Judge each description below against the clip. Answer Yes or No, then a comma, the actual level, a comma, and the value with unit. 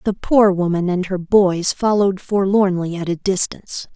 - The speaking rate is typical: Yes, average, 165 wpm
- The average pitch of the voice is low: No, high, 190 Hz